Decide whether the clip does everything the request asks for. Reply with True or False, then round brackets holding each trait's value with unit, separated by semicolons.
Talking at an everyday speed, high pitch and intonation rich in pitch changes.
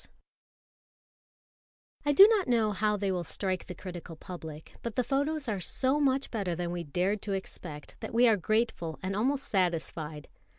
True (175 wpm; 200 Hz; 5.8 semitones)